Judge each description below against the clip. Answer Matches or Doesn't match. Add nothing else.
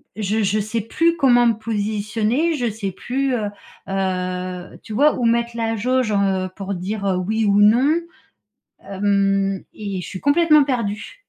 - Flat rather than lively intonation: Doesn't match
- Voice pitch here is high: Matches